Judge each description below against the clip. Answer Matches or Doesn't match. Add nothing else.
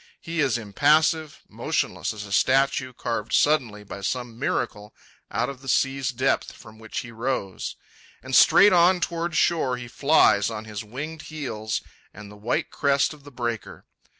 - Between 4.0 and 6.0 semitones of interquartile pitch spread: Matches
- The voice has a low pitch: Matches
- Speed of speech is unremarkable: Matches